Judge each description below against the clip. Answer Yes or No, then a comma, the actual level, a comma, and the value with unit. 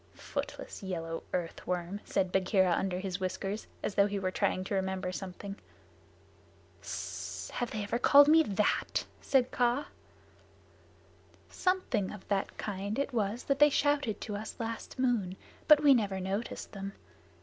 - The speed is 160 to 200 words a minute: No, average, 150 wpm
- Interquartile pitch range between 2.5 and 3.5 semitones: No, average, 4.4 semitones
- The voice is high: Yes, high, 205 Hz